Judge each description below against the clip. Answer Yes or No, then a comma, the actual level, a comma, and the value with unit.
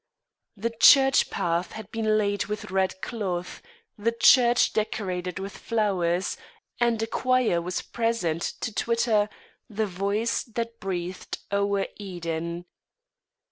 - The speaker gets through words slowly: Yes, slow, 120 wpm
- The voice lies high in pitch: Yes, high, 205 Hz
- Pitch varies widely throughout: No, average, 4.0 semitones